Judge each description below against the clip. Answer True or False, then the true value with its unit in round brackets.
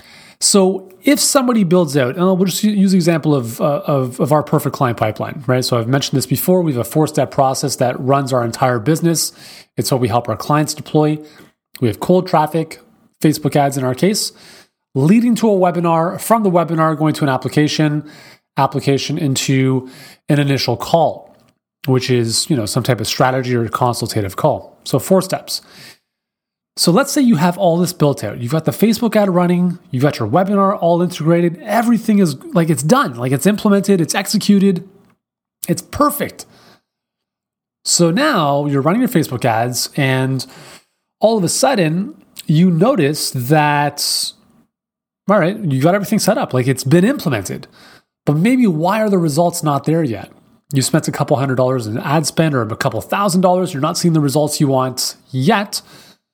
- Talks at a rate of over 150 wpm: True (180 wpm)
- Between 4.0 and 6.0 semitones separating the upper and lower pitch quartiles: True (5.6 semitones)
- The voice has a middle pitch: True (155 Hz)